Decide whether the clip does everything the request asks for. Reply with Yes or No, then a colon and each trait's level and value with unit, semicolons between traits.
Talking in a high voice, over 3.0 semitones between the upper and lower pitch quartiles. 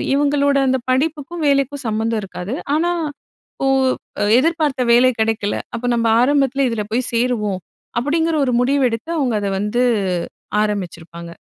Yes: very high, 250 Hz; average, 4.4 semitones